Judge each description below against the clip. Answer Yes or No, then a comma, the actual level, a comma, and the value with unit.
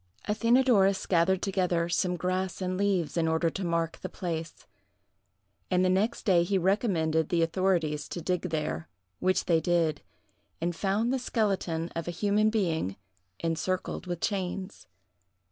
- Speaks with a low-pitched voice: No, medium, 180 Hz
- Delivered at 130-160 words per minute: Yes, average, 145 wpm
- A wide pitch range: No, average, 2.8 semitones